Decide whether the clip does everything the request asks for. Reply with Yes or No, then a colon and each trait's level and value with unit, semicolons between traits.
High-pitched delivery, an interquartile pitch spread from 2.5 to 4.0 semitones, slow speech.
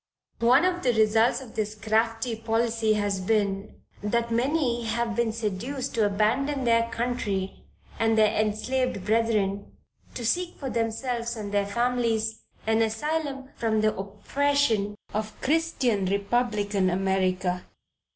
Yes: high, 225 Hz; average, 2.8 semitones; slow, 130 wpm